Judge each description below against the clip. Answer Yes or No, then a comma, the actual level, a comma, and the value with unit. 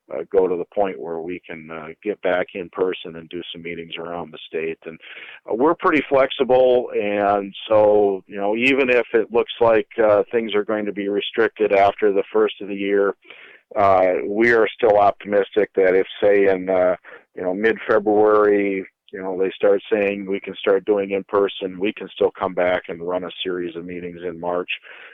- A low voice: Yes, low, 100 Hz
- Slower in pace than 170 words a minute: No, fast, 205 wpm